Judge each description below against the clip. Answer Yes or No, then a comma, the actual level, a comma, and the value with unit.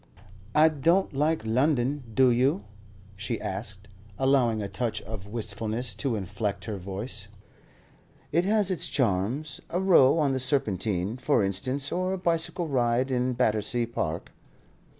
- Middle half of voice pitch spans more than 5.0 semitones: Yes, wide, 5.4 semitones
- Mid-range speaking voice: No, low, 120 Hz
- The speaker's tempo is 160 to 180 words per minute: No, average, 140 wpm